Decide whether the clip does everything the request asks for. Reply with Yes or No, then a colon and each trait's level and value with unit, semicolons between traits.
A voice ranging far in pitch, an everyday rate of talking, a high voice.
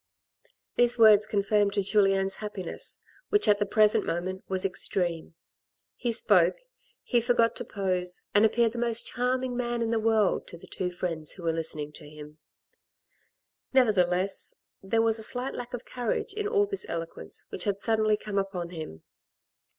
No: average, 4.4 semitones; average, 165 wpm; high, 205 Hz